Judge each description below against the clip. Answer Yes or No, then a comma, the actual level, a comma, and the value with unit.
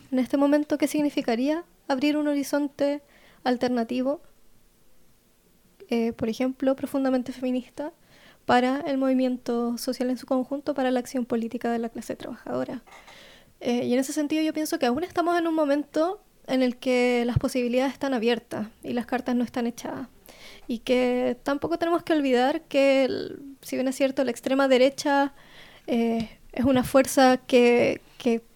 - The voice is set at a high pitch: Yes, very high, 265 Hz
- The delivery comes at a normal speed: Yes, average, 160 wpm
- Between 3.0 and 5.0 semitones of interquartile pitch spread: No, narrow, 2.6 semitones